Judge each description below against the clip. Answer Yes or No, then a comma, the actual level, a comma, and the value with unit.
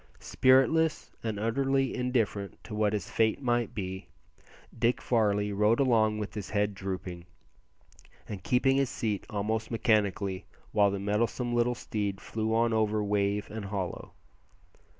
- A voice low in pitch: Yes, low, 110 Hz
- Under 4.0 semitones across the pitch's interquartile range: Yes, average, 2.7 semitones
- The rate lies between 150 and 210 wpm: No, average, 140 wpm